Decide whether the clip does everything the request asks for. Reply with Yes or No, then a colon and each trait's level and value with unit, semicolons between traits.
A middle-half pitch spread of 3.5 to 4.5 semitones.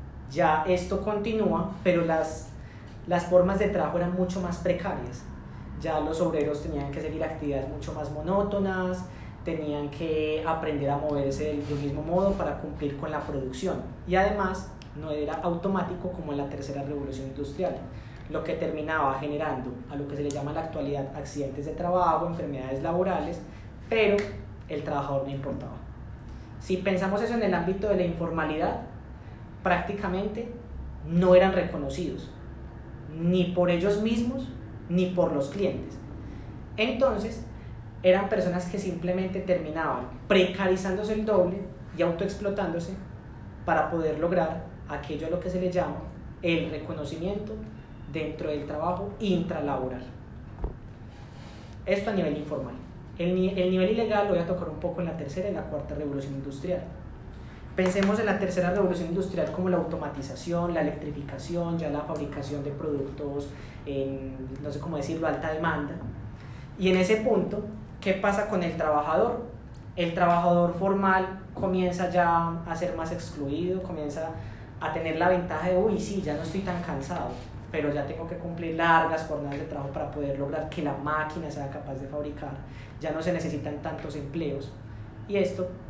Yes: average, 4.1 semitones